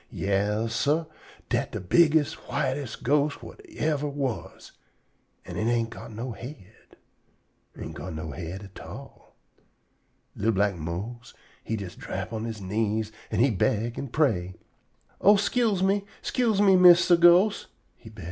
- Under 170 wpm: Yes, average, 145 wpm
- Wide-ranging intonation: Yes, wide, 7.4 semitones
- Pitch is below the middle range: Yes, low, 120 Hz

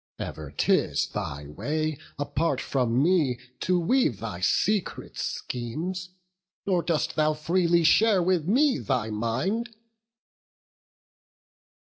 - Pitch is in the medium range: Yes, medium, 155 Hz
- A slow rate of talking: Yes, slow, 105 wpm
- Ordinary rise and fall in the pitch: No, wide, 6.9 semitones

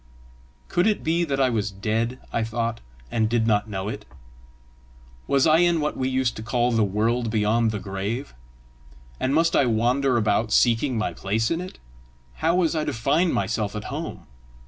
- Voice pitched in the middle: No, low, 115 Hz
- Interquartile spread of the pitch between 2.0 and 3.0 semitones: No, average, 4.2 semitones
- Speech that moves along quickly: No, average, 185 wpm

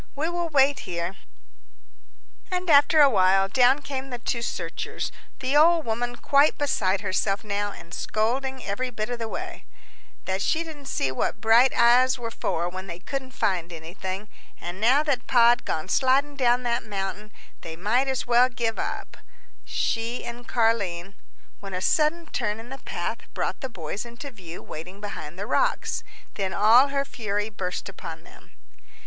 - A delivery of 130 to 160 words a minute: No, average, 170 wpm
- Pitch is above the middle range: Yes, high, 235 Hz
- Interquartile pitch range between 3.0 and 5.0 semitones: No, wide, 5.5 semitones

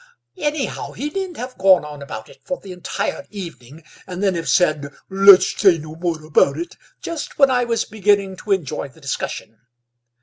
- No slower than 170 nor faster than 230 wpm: Yes, average, 180 wpm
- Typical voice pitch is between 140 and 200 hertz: Yes, medium, 185 Hz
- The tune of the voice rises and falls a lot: Yes, wide, 5.7 semitones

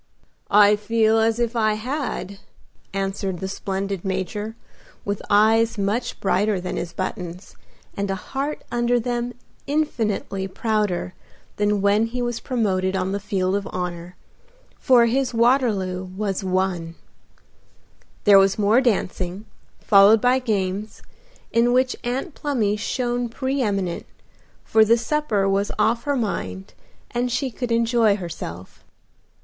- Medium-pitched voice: No, high, 210 Hz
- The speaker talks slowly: Yes, slow, 130 wpm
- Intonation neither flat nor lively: Yes, average, 3.7 semitones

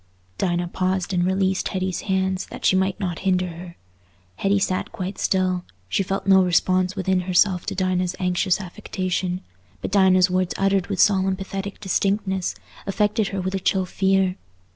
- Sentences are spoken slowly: No, average, 165 wpm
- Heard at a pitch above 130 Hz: Yes, high, 190 Hz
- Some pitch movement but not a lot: No, narrow, 1.0 semitones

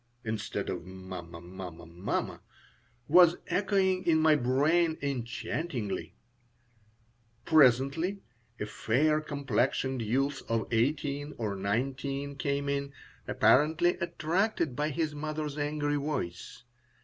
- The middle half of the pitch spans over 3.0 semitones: Yes, average, 5.0 semitones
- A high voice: No, medium, 140 Hz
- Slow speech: Yes, slow, 100 wpm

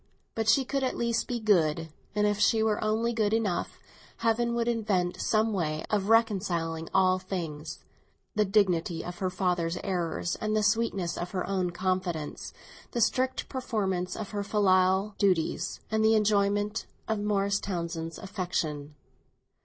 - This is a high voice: Yes, high, 200 Hz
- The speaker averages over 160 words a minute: No, average, 150 wpm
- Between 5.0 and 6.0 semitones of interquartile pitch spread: No, average, 3.5 semitones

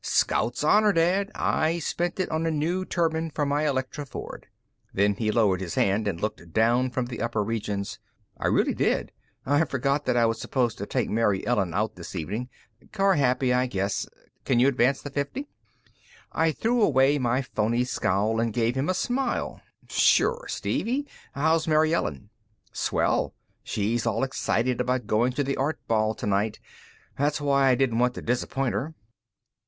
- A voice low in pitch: Yes, low, 125 Hz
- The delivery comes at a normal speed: Yes, average, 170 wpm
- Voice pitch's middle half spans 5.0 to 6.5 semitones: Yes, wide, 5.4 semitones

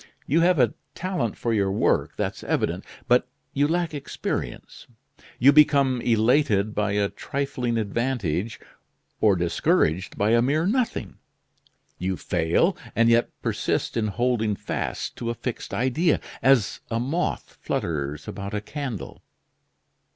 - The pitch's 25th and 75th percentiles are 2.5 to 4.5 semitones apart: No, wide, 5.5 semitones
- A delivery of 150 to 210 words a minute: No, slow, 135 wpm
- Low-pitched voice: Yes, low, 115 Hz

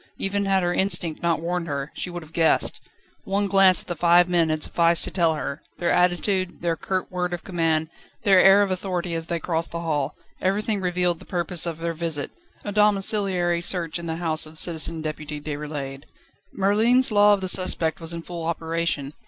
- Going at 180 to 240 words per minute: Yes, average, 200 wpm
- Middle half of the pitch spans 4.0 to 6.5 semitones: No, narrow, 2.5 semitones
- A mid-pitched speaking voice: Yes, medium, 175 Hz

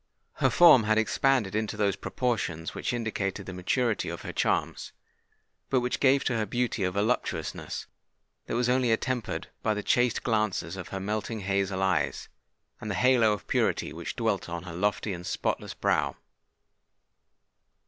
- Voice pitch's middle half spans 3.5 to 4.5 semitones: Yes, average, 4.1 semitones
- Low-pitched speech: Yes, low, 110 Hz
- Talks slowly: No, average, 160 wpm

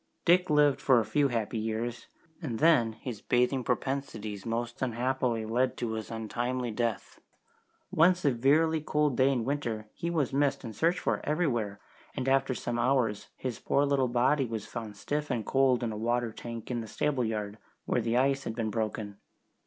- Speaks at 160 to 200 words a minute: Yes, average, 180 wpm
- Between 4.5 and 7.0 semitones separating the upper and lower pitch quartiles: No, average, 3.5 semitones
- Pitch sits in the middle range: No, low, 120 Hz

